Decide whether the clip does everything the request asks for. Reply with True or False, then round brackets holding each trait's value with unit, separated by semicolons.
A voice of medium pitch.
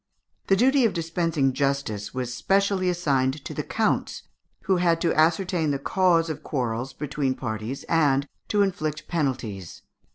True (155 Hz)